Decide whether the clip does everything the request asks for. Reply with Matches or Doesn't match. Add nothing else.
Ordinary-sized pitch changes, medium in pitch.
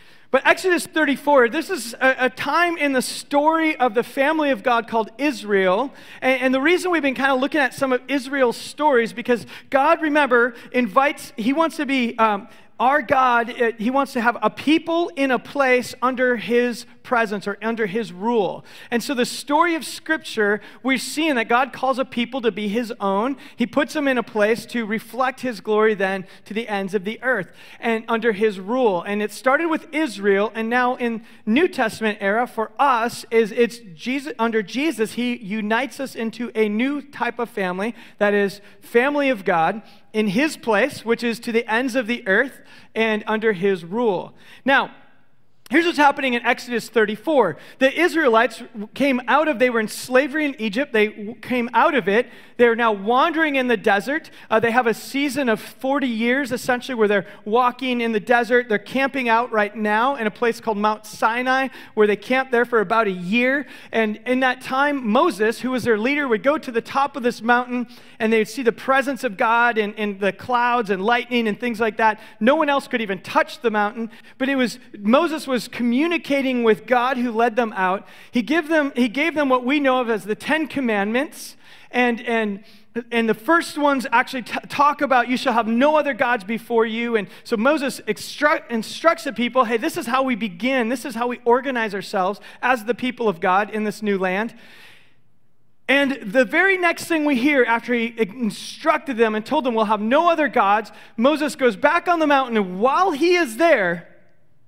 Doesn't match